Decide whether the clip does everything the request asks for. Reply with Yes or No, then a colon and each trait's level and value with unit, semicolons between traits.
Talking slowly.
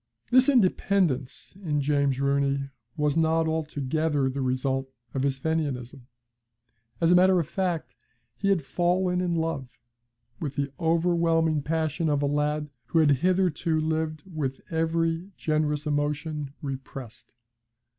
Yes: slow, 130 wpm